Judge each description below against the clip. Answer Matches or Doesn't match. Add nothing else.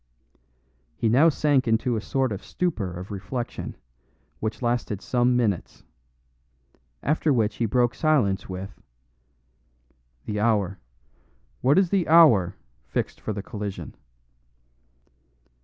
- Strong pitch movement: Doesn't match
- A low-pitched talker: Matches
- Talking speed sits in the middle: Doesn't match